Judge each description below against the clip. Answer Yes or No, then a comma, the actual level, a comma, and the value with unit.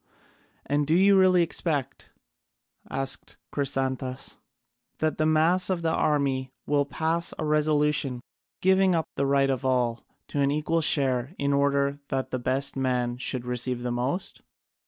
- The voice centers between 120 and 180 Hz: Yes, medium, 140 Hz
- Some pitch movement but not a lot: Yes, average, 3.2 semitones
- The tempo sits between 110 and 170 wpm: Yes, average, 150 wpm